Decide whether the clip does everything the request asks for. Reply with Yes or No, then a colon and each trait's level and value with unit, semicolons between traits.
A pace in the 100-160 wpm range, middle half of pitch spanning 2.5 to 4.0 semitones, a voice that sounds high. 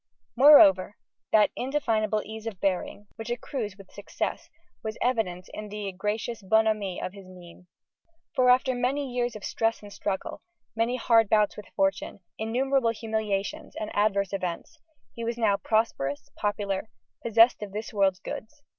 Yes: average, 150 wpm; average, 2.9 semitones; high, 215 Hz